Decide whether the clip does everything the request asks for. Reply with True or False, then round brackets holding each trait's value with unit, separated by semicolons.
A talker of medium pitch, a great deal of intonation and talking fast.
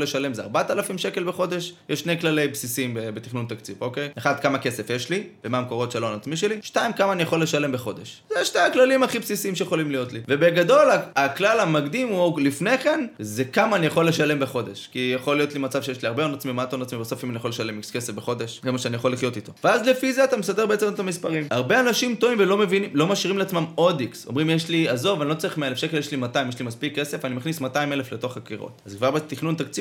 True (145 Hz; 7.0 semitones; 190 wpm)